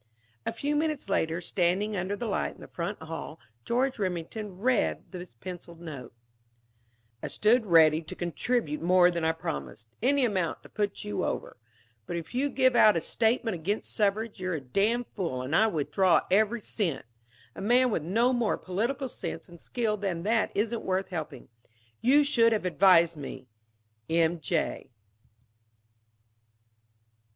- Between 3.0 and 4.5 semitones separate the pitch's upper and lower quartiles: No, wide, 5.5 semitones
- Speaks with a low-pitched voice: No, high, 195 Hz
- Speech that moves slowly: No, average, 160 wpm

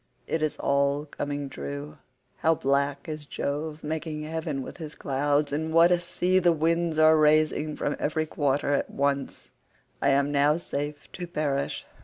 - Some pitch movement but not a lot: No, narrow, 1.9 semitones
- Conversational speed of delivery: Yes, average, 165 wpm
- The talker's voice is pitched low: No, medium, 150 Hz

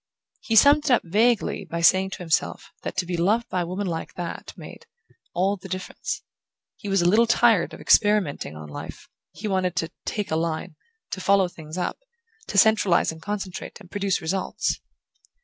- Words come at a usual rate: Yes, average, 185 wpm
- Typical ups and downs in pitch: Yes, average, 3.3 semitones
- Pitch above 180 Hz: Yes, high, 190 Hz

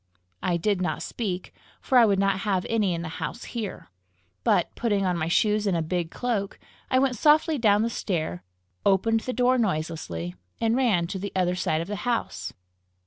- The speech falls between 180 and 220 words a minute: Yes, average, 195 wpm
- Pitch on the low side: No, high, 200 Hz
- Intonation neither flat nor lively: Yes, average, 4.7 semitones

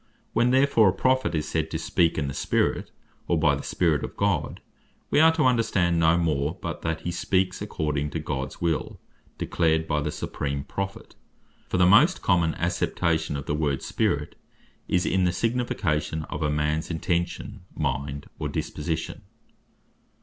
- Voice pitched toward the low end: Yes, very low, 85 Hz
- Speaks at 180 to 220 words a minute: No, average, 165 wpm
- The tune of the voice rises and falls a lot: No, average, 3.7 semitones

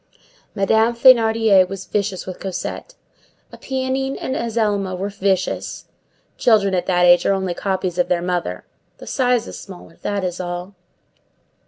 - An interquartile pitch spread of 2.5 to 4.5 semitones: Yes, average, 3.7 semitones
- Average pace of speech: Yes, average, 145 wpm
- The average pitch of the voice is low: No, high, 195 Hz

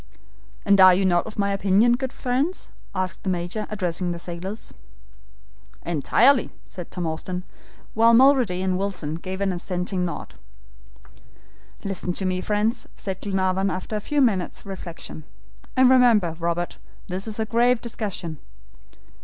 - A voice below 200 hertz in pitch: Yes, high, 190 Hz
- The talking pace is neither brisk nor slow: Yes, average, 145 wpm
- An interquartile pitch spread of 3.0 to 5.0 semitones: Yes, average, 3.7 semitones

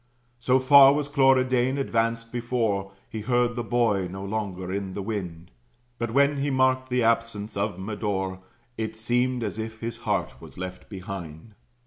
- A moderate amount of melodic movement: Yes, average, 4.3 semitones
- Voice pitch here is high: No, low, 115 Hz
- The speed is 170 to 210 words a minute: No, average, 160 wpm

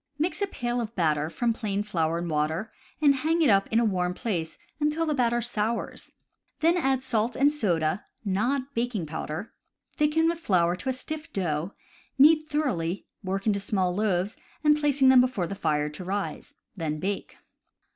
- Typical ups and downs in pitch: No, wide, 7.1 semitones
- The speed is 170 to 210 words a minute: Yes, average, 175 wpm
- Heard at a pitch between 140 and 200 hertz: No, high, 215 Hz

